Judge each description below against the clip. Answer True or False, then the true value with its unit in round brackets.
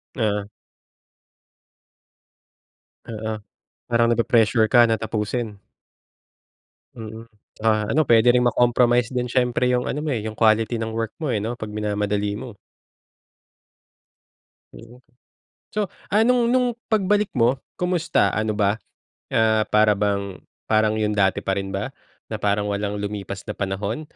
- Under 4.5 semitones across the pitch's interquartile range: True (2.9 semitones)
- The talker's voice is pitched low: True (110 Hz)